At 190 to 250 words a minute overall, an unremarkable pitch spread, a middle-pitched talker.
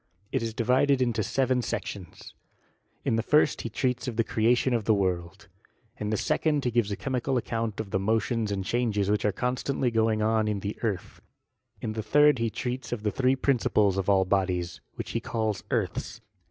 No: average, 200 wpm; average, 3.4 semitones; low, 110 Hz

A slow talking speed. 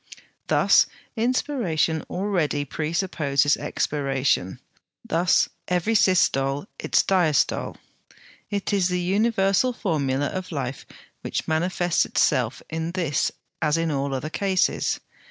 Yes: slow, 105 wpm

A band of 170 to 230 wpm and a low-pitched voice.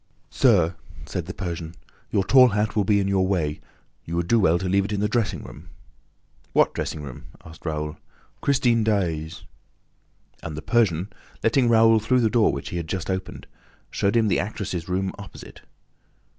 Yes: average, 180 wpm; very low, 95 Hz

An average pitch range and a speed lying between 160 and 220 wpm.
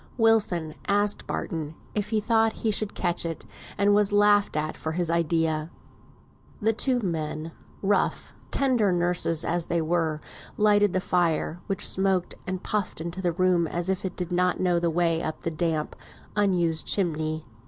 Yes: average, 3.8 semitones; average, 165 wpm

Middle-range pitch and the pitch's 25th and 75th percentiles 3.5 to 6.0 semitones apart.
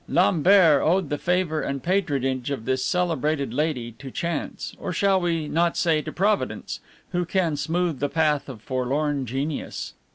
Yes: medium, 155 Hz; average, 4.1 semitones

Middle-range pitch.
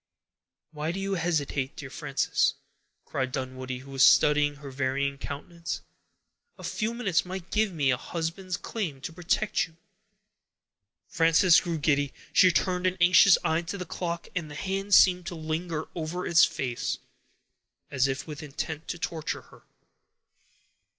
Yes: medium, 165 Hz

